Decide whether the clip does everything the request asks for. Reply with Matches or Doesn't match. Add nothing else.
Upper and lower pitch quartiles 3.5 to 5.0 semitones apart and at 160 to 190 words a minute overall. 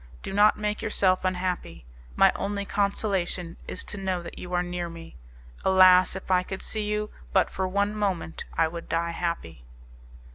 Doesn't match